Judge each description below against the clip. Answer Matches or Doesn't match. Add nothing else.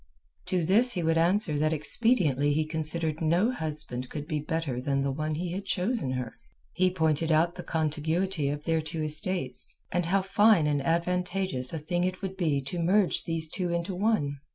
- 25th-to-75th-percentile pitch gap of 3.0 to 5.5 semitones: Matches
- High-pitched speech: Doesn't match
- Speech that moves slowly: Doesn't match